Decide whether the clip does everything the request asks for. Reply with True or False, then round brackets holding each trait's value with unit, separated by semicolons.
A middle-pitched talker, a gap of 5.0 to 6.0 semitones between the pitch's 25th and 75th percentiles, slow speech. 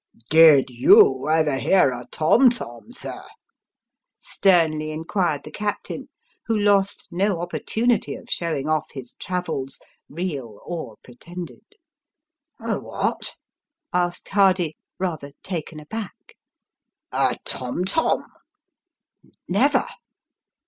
True (170 Hz; 5.3 semitones; 120 wpm)